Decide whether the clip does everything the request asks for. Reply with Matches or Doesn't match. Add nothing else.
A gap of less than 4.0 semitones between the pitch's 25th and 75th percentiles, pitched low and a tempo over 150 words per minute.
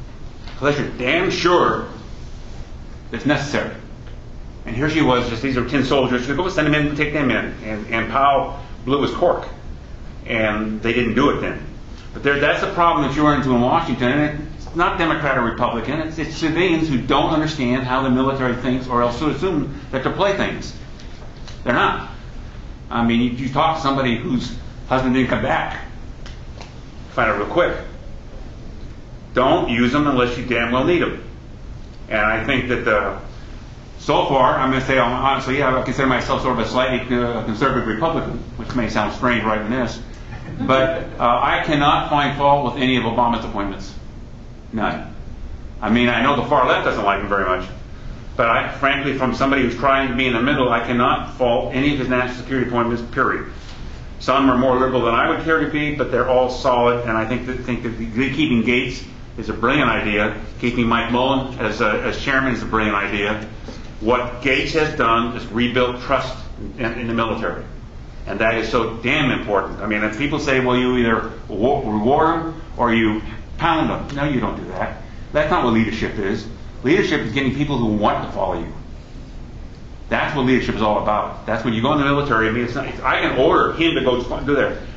Matches